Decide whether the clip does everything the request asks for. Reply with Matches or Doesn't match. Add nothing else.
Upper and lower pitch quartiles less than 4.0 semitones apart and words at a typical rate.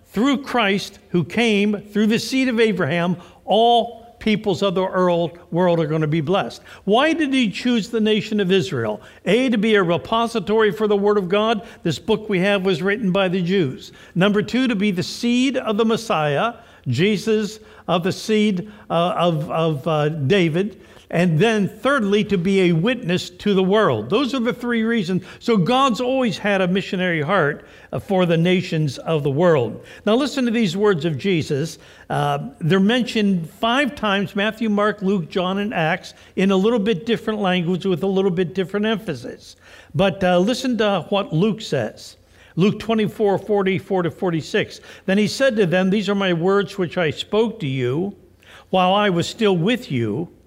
Matches